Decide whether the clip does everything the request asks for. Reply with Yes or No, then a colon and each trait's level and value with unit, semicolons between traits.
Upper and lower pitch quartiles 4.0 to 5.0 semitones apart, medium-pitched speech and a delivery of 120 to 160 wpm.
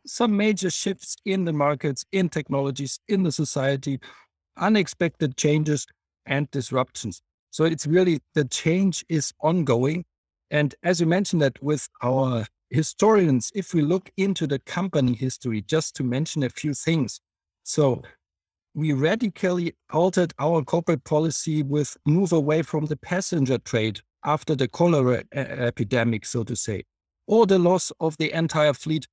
Yes: average, 4.6 semitones; medium, 150 Hz; average, 145 wpm